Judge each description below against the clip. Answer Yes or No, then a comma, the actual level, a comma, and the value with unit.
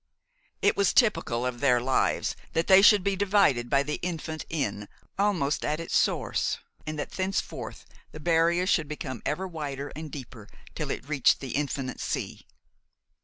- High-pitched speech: No, medium, 150 Hz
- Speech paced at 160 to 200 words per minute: Yes, average, 165 wpm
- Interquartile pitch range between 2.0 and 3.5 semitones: No, average, 5.1 semitones